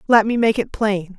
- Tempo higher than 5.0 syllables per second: No, 4.9 syllables/s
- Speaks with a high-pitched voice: Yes, high, 215 Hz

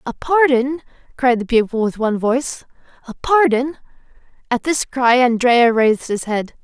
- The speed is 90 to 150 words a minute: Yes, average, 145 wpm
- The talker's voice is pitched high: Yes, very high, 250 Hz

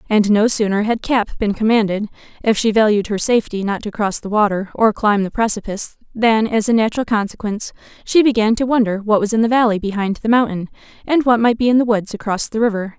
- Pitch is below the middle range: No, high, 215 Hz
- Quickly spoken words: Yes, fast, 220 wpm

